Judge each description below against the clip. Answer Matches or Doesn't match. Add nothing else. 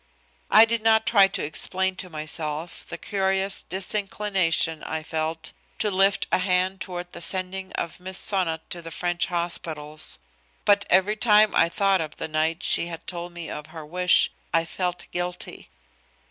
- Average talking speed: Matches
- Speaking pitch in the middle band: Matches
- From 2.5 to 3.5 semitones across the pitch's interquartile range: Matches